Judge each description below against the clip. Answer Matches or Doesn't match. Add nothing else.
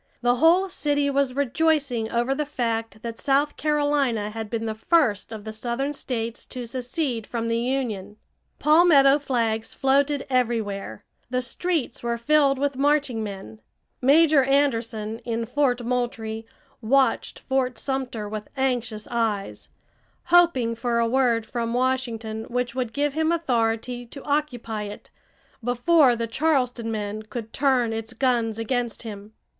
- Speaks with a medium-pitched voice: Doesn't match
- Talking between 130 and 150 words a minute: Matches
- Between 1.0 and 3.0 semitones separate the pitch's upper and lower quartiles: Doesn't match